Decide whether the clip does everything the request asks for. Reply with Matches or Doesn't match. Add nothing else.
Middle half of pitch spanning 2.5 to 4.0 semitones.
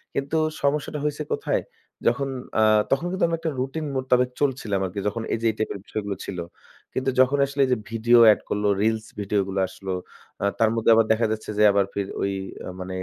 Doesn't match